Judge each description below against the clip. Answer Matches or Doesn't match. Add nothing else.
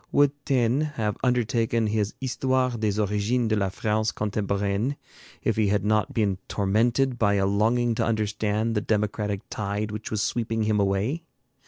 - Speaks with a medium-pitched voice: Doesn't match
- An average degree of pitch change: Doesn't match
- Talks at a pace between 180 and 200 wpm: Doesn't match